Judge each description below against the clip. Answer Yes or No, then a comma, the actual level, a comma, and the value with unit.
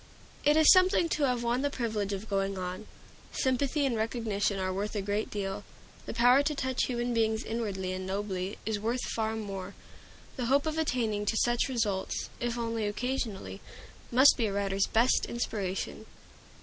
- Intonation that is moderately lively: Yes, average, 3.8 semitones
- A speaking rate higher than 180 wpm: No, average, 175 wpm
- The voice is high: Yes, high, 225 Hz